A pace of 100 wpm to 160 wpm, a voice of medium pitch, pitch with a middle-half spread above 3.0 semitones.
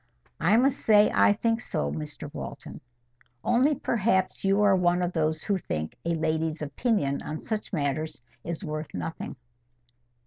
Yes: average, 150 wpm; medium, 175 Hz; average, 5.3 semitones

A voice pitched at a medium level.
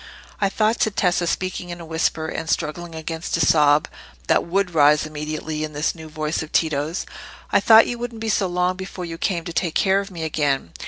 Yes: medium, 165 Hz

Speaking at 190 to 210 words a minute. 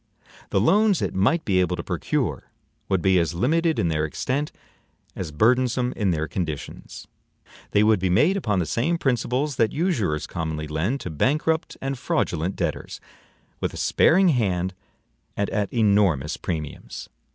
No: average, 155 wpm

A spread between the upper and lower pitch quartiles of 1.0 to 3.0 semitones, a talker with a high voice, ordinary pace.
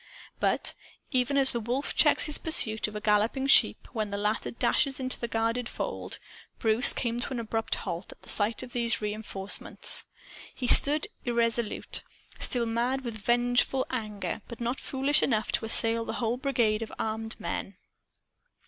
Yes: narrow, 2.5 semitones; high, 235 Hz; average, 165 wpm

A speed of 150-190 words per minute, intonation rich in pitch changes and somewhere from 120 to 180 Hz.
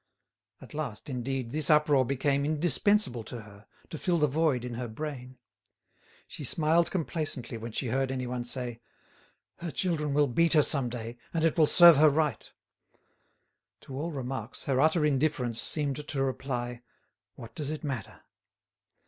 No: average, 155 wpm; average, 3.8 semitones; medium, 140 Hz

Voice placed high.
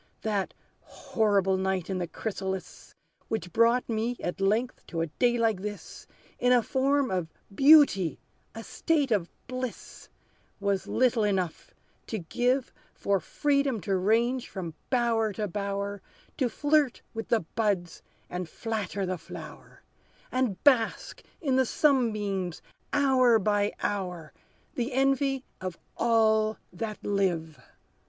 Yes: high, 215 Hz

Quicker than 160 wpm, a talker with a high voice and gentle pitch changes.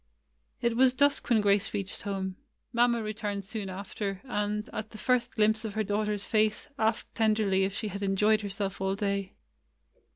Yes: average, 170 wpm; high, 210 Hz; narrow, 1.7 semitones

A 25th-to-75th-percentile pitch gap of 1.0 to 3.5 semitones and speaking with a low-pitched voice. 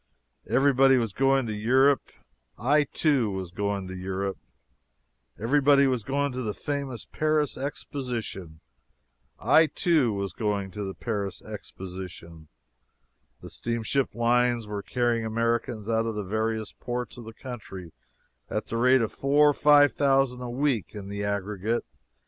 No: average, 4.8 semitones; low, 115 Hz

